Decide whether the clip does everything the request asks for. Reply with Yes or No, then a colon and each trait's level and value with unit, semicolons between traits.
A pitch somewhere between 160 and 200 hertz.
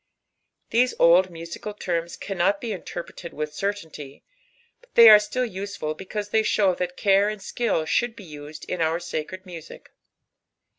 Yes: medium, 185 Hz